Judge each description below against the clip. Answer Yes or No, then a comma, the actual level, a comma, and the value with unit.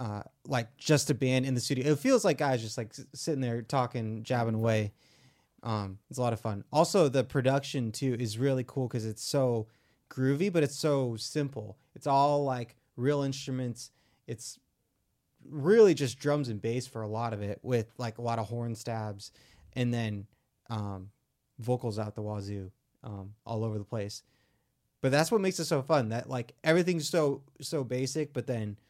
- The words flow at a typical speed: Yes, average, 185 wpm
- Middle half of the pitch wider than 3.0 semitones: Yes, average, 3.8 semitones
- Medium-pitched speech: No, low, 125 Hz